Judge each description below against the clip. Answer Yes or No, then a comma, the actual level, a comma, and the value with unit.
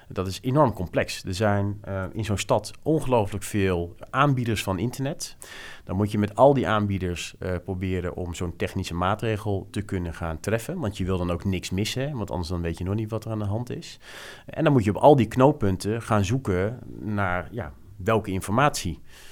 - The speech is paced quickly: Yes, fast, 205 wpm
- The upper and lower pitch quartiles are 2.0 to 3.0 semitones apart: No, average, 3.9 semitones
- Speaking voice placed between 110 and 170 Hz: No, low, 100 Hz